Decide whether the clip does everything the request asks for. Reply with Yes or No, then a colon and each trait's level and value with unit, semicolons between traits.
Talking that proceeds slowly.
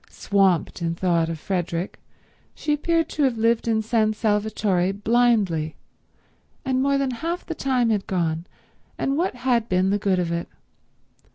No: average, 160 wpm